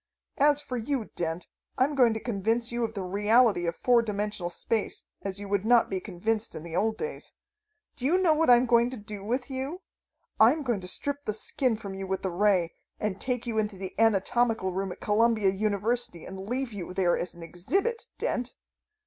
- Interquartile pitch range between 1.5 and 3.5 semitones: No, average, 4.2 semitones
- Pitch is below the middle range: No, high, 220 Hz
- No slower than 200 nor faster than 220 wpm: Yes, fast, 205 wpm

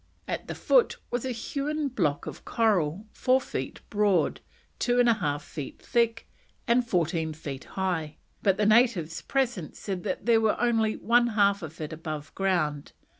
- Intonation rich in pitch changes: Yes, wide, 6.8 semitones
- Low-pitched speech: No, high, 205 Hz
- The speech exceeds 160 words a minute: Yes, average, 170 wpm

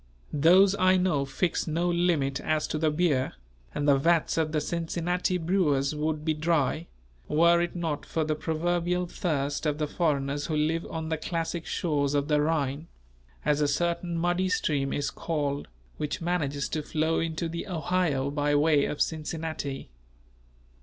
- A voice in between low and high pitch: Yes, medium, 160 Hz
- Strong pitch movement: No, average, 2.7 semitones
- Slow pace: No, average, 165 wpm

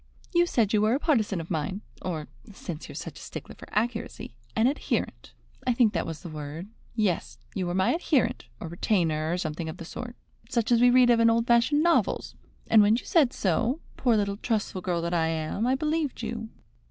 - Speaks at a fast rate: Yes, fast, 215 wpm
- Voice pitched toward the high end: Yes, high, 215 Hz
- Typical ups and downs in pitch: No, wide, 6.0 semitones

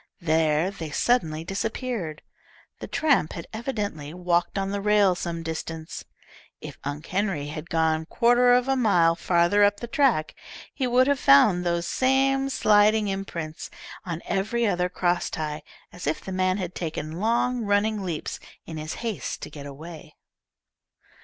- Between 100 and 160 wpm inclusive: Yes, average, 155 wpm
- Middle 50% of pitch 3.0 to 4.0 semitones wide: No, average, 5.3 semitones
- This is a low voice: No, medium, 185 Hz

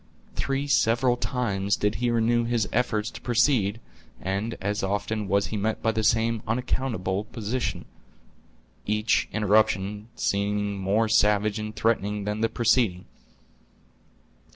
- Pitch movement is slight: Yes, narrow, 2.1 semitones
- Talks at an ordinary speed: No, slow, 130 wpm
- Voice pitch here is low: Yes, low, 110 Hz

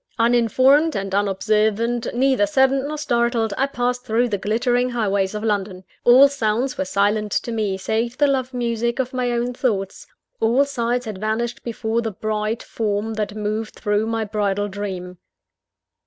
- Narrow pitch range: No, average, 3.0 semitones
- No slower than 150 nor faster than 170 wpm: Yes, average, 160 wpm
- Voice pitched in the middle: No, high, 225 Hz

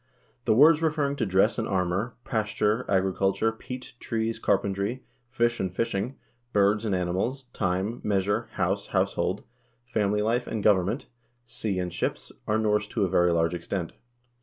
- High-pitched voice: No, low, 105 Hz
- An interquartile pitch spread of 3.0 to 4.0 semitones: Yes, average, 3.6 semitones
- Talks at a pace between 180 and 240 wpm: No, average, 155 wpm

